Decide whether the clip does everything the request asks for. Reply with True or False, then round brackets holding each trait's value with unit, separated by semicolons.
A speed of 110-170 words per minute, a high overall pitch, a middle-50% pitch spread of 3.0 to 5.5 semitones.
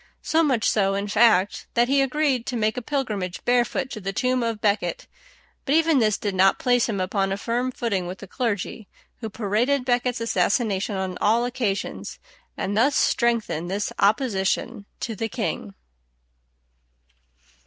True (165 wpm; 225 Hz; 3.9 semitones)